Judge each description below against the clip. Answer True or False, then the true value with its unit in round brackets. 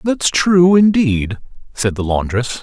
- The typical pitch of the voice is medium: True (145 Hz)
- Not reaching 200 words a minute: True (135 wpm)